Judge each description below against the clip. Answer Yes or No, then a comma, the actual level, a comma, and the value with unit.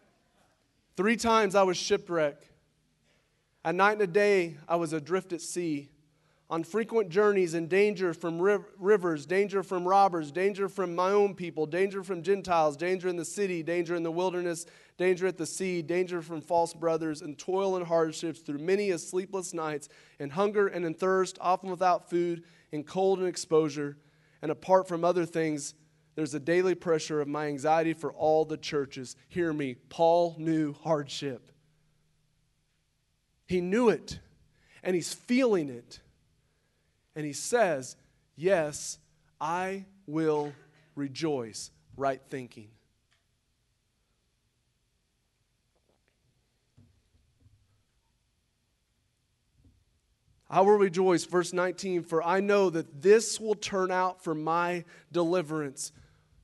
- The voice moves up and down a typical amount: Yes, average, 3.7 semitones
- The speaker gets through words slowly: Yes, slow, 130 wpm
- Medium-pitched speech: Yes, medium, 165 Hz